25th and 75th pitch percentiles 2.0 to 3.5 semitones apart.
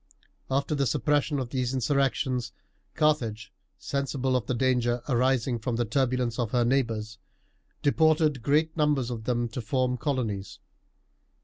Yes: average, 2.8 semitones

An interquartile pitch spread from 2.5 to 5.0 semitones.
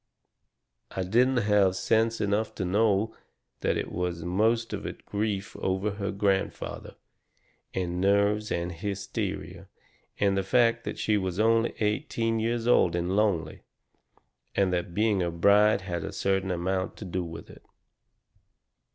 Yes: average, 2.8 semitones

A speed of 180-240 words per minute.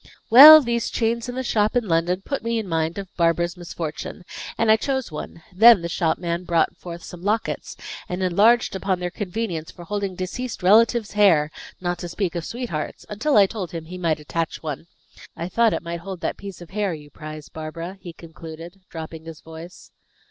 Yes: average, 195 wpm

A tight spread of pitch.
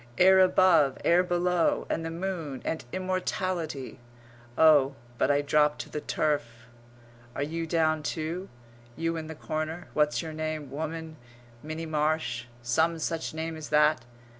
Yes: narrow, 1.9 semitones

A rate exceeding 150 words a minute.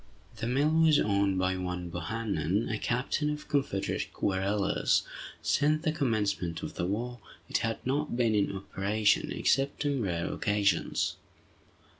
No: average, 140 wpm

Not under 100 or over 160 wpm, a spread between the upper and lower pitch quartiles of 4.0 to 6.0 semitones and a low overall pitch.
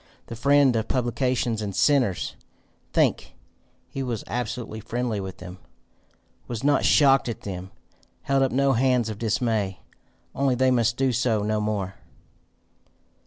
No: average, 140 wpm; average, 3.4 semitones; low, 120 Hz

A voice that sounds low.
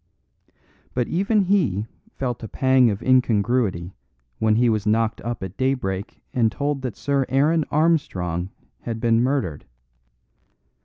Yes: low, 120 Hz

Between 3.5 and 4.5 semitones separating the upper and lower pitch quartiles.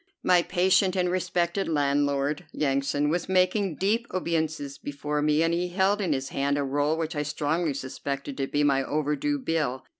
Yes: average, 3.9 semitones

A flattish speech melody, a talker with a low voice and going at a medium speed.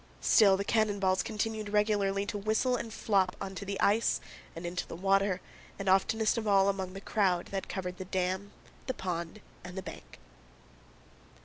No: narrow, 2.0 semitones; high, 195 Hz; average, 175 wpm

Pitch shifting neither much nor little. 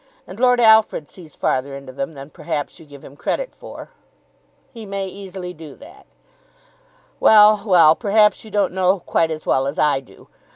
No: wide, 6.2 semitones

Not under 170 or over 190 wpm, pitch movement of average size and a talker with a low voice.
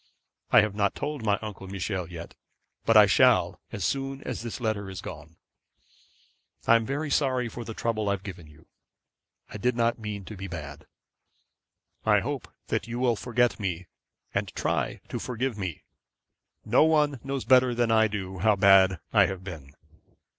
Yes: average, 175 wpm; average, 4.5 semitones; low, 105 Hz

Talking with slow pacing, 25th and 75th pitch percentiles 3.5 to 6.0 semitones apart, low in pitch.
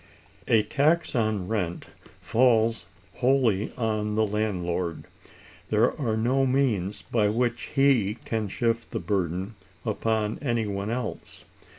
No: slow, 120 wpm; average, 2.8 semitones; low, 110 Hz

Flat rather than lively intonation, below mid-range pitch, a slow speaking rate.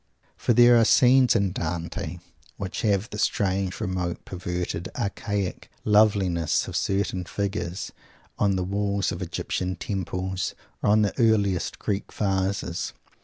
Yes: narrow, 2.2 semitones; low, 100 Hz; slow, 130 wpm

